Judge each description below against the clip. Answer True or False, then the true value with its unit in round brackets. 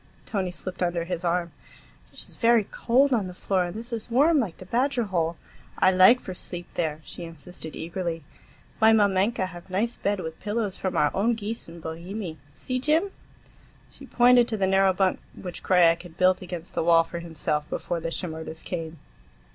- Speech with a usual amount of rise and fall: True (4.6 semitones)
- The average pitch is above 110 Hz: True (185 Hz)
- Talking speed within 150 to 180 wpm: False (190 wpm)